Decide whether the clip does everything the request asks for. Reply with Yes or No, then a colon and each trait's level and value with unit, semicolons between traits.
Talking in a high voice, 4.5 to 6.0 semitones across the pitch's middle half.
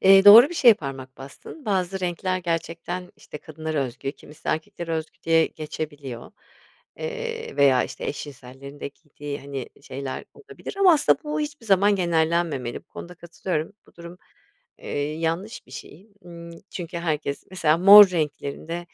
No: medium, 165 Hz; average, 4.8 semitones